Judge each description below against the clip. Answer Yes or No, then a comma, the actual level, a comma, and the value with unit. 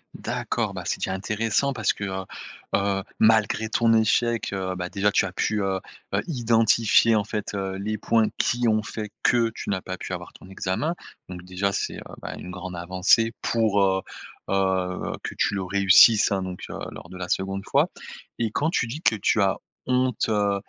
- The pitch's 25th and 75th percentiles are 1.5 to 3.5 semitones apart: Yes, average, 3.1 semitones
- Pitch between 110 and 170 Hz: No, low, 100 Hz